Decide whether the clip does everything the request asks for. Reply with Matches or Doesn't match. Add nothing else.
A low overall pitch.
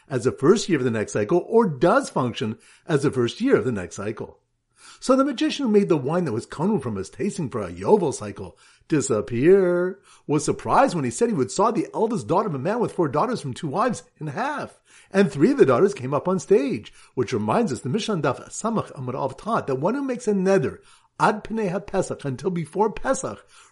Doesn't match